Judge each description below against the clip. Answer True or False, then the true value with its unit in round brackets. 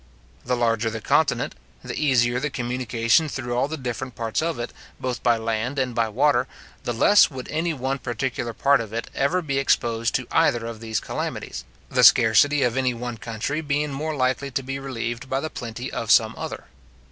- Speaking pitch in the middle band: False (125 Hz)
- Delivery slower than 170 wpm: False (195 wpm)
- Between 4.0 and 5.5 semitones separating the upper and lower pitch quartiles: False (3.0 semitones)